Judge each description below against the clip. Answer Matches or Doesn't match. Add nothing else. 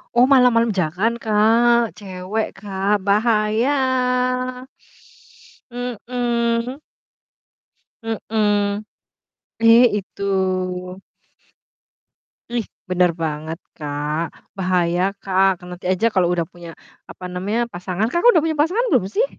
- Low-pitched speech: Doesn't match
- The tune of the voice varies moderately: Matches